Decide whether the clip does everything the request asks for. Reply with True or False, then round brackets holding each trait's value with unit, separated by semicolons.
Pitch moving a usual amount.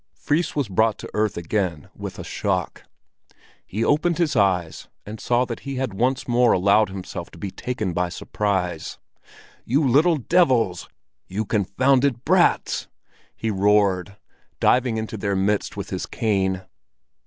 True (5.0 semitones)